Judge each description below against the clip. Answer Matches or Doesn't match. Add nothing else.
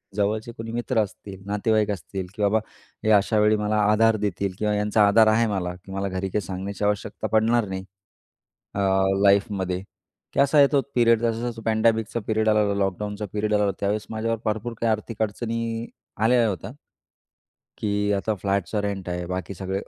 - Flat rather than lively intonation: Matches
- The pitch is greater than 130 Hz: Doesn't match